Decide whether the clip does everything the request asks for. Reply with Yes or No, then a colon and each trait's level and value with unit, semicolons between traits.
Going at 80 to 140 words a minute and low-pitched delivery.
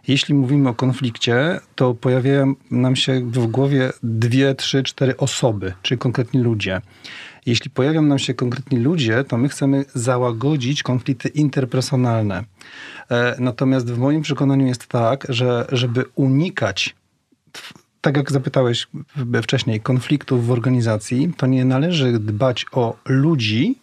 Yes: average, 130 wpm; low, 130 Hz